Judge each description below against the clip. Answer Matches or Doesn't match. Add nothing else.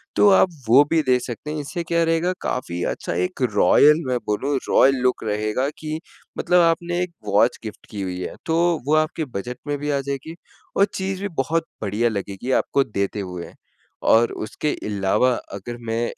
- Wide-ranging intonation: Matches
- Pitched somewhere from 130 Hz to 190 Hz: Matches